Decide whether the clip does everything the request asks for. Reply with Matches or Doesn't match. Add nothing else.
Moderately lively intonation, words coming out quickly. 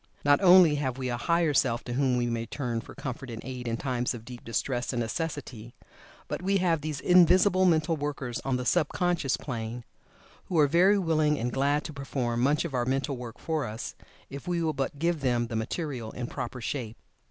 Matches